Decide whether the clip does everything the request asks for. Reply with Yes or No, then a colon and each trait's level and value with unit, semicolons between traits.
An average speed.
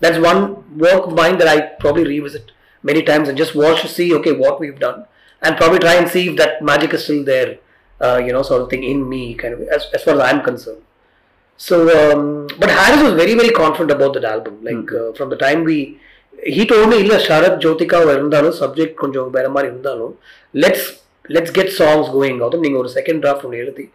No: fast, 190 wpm